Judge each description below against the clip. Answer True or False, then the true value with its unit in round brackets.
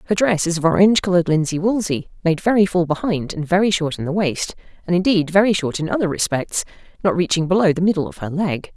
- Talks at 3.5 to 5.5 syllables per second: False (6.3 syllables/s)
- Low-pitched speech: False (180 Hz)